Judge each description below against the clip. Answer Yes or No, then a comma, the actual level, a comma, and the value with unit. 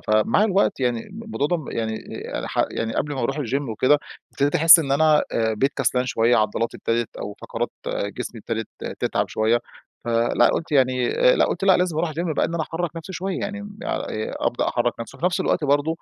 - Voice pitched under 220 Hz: Yes, medium, 140 Hz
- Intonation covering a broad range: Yes, wide, 6.5 semitones